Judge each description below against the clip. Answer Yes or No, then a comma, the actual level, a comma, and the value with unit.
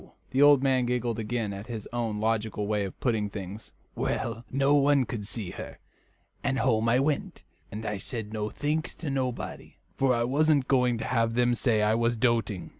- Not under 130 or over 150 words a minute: No, average, 190 wpm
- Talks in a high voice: No, low, 120 Hz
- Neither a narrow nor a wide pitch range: Yes, average, 3.2 semitones